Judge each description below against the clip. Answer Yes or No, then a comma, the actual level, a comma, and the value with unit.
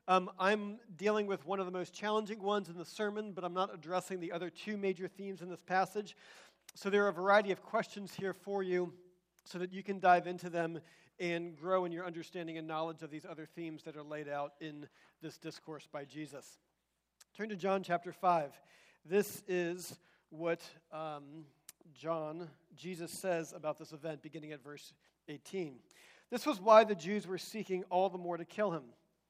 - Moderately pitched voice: Yes, medium, 180 Hz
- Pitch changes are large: No, average, 3.2 semitones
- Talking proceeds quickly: No, average, 195 wpm